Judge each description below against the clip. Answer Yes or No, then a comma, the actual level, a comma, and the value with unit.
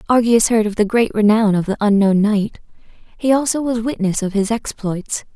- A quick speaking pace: No, average, 190 wpm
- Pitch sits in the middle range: No, high, 215 Hz